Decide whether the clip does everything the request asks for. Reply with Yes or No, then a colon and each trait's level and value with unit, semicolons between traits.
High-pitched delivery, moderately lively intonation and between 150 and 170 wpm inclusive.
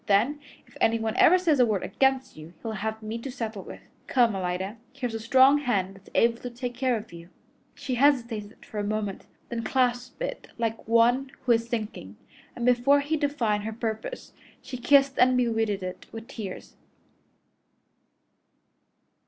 Yes: high, 230 Hz; average, 3.2 semitones; average, 165 wpm